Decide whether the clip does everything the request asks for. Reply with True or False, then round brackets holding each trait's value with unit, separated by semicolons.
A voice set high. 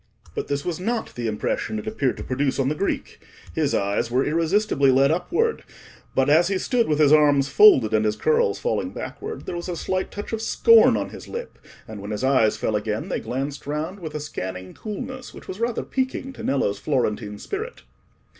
False (150 Hz)